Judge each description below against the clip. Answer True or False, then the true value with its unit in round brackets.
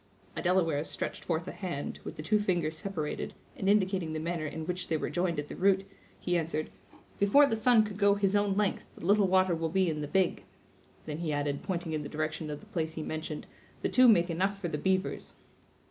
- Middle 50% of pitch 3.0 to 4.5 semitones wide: True (3.8 semitones)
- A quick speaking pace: True (225 wpm)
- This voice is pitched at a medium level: True (175 Hz)